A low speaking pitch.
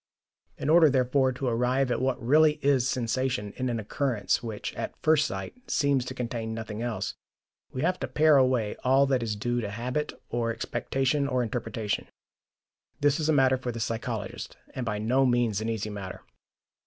Yes: low, 125 Hz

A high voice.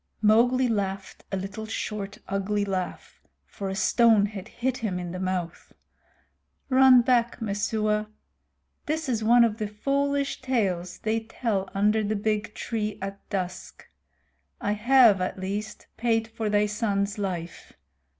Yes: high, 210 Hz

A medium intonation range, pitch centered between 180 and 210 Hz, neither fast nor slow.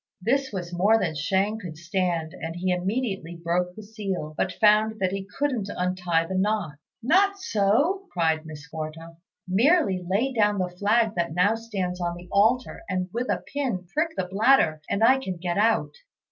Yes: average, 4.2 semitones; high, 190 Hz; average, 180 wpm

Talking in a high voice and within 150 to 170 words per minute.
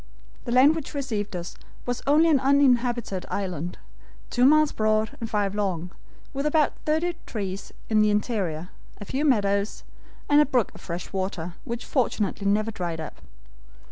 Yes: high, 215 Hz; average, 160 wpm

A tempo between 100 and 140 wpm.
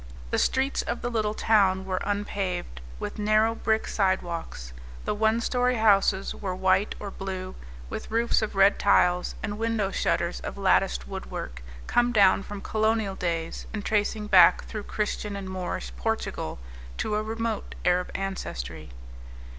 No: average, 150 wpm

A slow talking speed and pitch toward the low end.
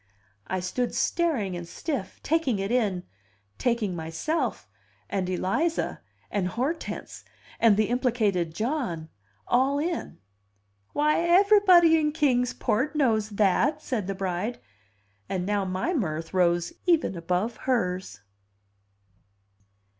No: slow, 115 wpm; high, 220 Hz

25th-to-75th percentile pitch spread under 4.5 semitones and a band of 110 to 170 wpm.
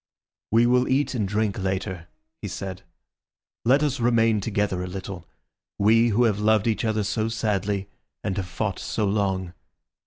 Yes: average, 2.9 semitones; average, 160 wpm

